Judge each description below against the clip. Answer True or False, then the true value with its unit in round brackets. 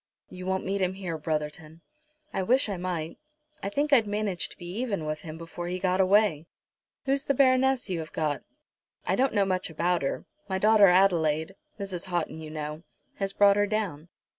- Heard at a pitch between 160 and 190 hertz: True (185 Hz)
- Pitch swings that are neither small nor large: True (4.1 semitones)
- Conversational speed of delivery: True (190 wpm)